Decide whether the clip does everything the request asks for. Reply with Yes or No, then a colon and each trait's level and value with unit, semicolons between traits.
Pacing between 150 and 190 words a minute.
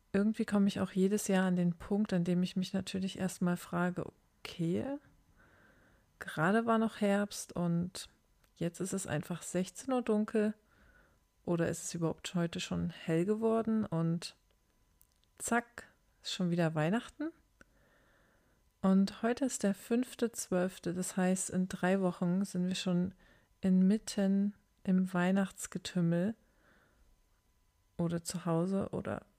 No: average, 130 wpm